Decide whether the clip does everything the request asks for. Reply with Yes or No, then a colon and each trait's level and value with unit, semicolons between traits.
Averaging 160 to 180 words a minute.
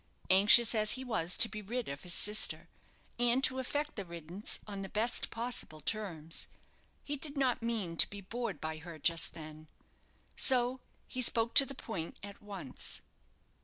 Yes: average, 170 wpm